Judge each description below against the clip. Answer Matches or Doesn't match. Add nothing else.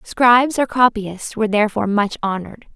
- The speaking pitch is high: Matches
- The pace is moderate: Matches